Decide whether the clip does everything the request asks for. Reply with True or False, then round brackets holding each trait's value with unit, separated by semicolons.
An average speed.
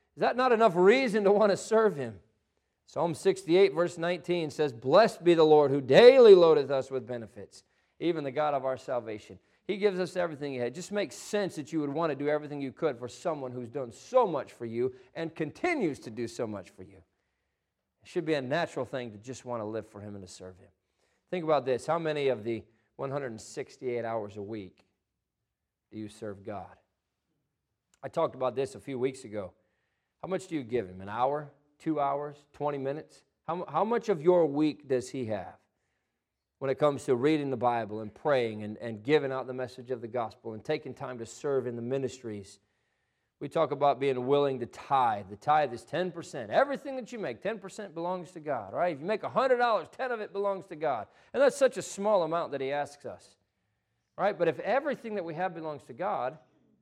False (215 wpm)